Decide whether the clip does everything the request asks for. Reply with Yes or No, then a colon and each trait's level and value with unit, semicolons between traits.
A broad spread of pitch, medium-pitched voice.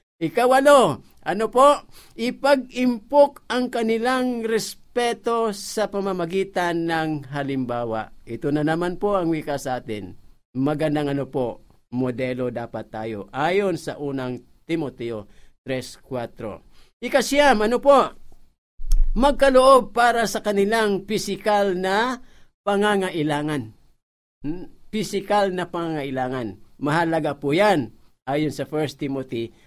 Yes: wide, 8.9 semitones; medium, 175 Hz